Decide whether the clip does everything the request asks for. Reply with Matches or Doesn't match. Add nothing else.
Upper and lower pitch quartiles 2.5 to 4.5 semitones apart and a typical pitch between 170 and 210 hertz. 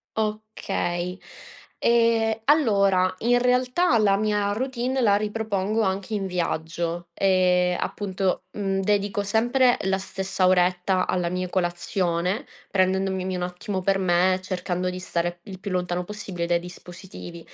Matches